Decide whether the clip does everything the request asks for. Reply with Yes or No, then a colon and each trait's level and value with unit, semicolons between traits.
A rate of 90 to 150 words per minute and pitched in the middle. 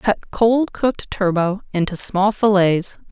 No: slow, 135 wpm; high, 200 Hz